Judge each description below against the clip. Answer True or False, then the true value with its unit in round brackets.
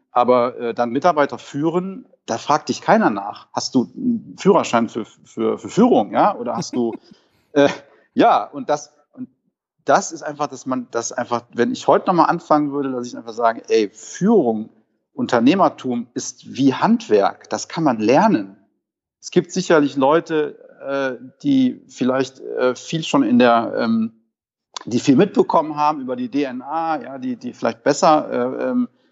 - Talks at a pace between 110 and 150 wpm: False (165 wpm)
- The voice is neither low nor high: True (145 Hz)